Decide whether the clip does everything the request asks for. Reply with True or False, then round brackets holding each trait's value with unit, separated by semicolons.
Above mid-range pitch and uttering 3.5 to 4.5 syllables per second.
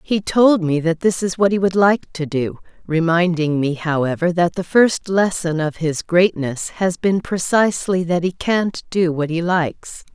False (175 Hz; 4.4 syllables/s)